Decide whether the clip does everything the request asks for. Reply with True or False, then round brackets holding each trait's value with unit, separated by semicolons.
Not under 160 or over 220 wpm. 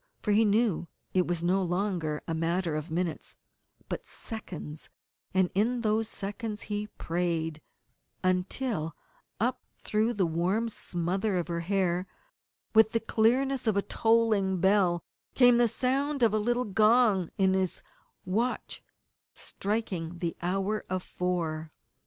False (140 wpm)